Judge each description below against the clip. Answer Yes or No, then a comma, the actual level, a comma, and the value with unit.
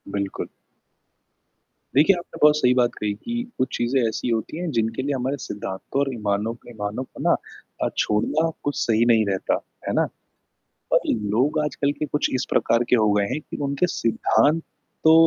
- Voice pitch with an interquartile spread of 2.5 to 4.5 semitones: No, average, 5.0 semitones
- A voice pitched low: Yes, low, 125 Hz